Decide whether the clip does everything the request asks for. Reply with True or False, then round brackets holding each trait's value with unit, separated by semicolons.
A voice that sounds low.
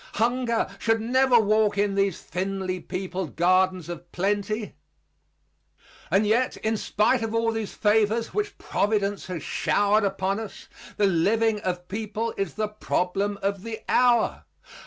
False (205 Hz)